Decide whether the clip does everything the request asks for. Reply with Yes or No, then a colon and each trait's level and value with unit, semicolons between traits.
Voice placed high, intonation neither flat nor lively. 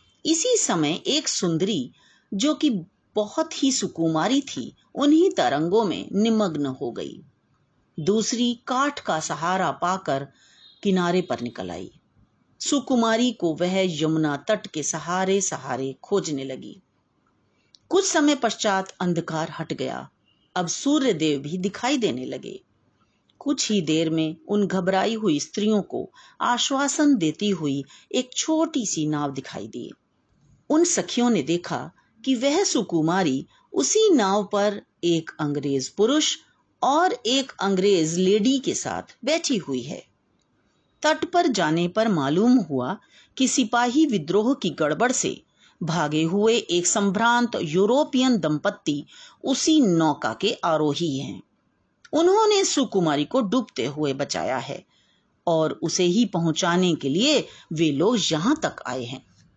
No: high, 200 Hz; wide, 8.6 semitones